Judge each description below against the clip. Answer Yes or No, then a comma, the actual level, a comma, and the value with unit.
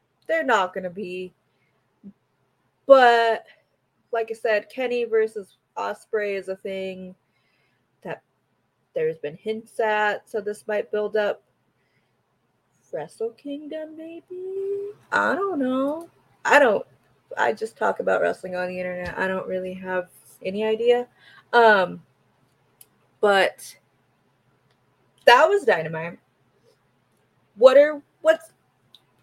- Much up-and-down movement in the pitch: Yes, wide, 7.5 semitones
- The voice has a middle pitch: No, high, 215 Hz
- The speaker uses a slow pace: Yes, slow, 110 wpm